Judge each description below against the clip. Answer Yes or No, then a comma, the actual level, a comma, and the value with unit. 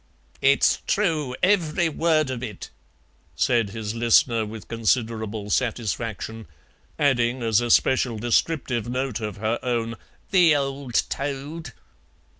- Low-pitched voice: Yes, low, 120 Hz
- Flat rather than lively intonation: No, average, 3.9 semitones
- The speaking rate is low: Yes, slow, 115 wpm